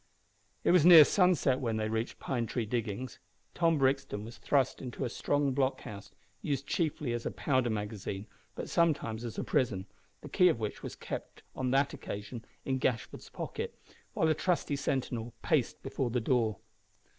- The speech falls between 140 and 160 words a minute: No, average, 170 wpm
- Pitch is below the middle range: Yes, low, 125 Hz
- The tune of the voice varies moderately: Yes, average, 4.1 semitones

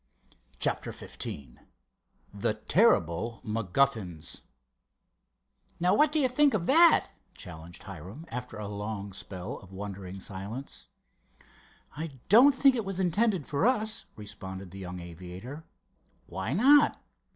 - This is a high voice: No, low, 110 Hz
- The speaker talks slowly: Yes, slow, 120 wpm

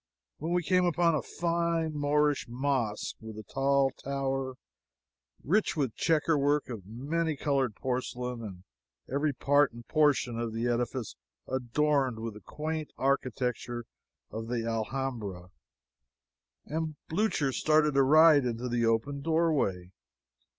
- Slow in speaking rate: Yes, slow, 130 wpm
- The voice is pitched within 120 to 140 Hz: Yes, low, 135 Hz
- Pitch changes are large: No, average, 4.4 semitones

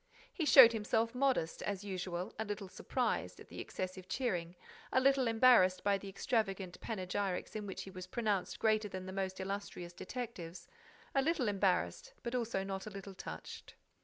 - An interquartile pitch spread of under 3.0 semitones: No, average, 3.7 semitones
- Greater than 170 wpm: No, average, 165 wpm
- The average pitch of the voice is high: Yes, high, 200 Hz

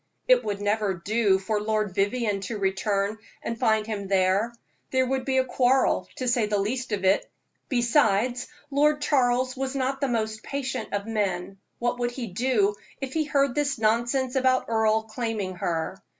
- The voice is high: Yes, high, 230 Hz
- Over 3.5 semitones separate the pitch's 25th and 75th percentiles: Yes, average, 4.1 semitones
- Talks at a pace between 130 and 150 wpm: No, average, 175 wpm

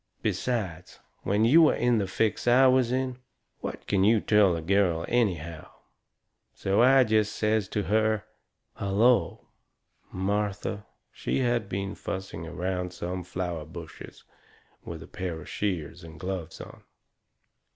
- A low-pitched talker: Yes, low, 100 Hz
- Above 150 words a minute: No, average, 140 wpm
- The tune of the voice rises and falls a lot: No, average, 3.9 semitones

